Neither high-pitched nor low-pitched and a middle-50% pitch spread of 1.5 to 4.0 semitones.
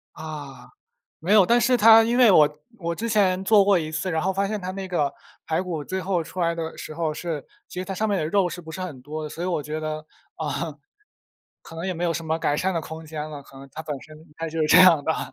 Yes: medium, 165 Hz; average, 3.5 semitones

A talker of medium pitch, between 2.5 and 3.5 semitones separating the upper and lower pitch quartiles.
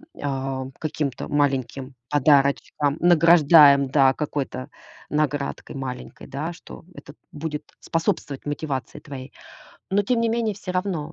Yes: medium, 145 Hz; average, 3.2 semitones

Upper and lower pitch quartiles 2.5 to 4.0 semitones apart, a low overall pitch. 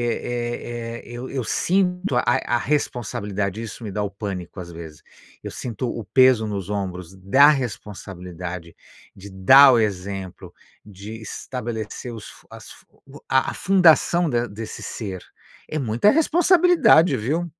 No: average, 5.1 semitones; low, 115 Hz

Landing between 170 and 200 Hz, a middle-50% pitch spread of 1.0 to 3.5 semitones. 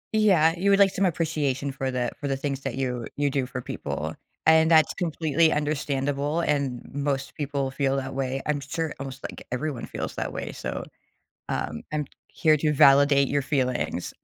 No: medium, 140 Hz; narrow, 2.5 semitones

